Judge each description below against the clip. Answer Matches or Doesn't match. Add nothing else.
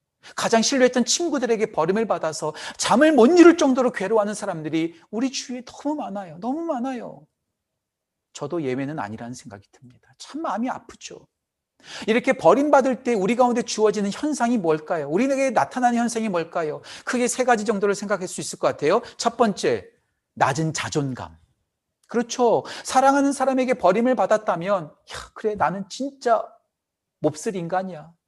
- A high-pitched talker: Matches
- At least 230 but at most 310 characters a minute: Doesn't match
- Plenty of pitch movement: Matches